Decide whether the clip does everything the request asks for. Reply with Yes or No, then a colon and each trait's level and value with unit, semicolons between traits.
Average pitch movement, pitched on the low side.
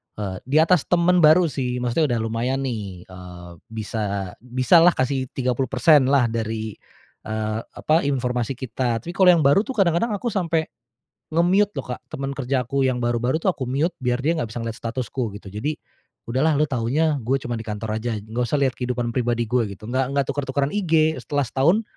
Yes: average, 4.9 semitones; low, 130 Hz